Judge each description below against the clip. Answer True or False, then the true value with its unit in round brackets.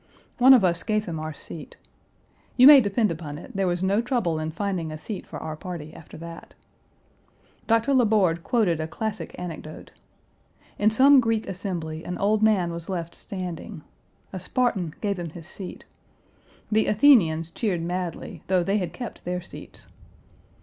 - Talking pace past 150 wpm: True (170 wpm)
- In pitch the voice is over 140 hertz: True (185 Hz)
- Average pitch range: True (4.5 semitones)